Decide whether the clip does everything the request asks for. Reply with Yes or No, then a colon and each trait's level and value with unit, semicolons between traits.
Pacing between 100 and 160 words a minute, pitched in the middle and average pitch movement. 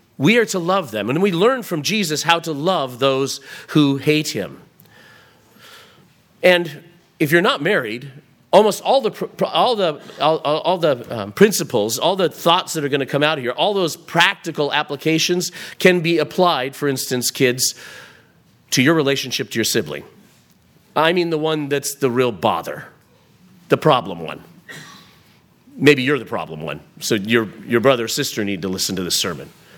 No: average, 175 wpm; medium, 150 Hz; average, 4.4 semitones